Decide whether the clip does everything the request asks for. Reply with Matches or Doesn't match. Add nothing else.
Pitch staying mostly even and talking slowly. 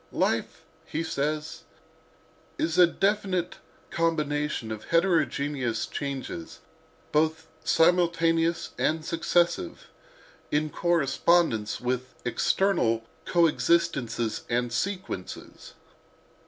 Doesn't match